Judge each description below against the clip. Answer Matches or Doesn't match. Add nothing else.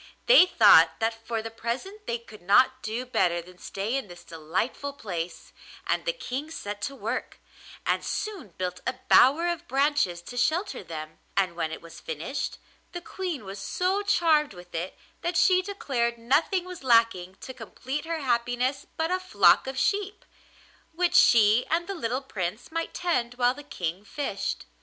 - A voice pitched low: Doesn't match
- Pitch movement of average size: Doesn't match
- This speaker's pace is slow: Doesn't match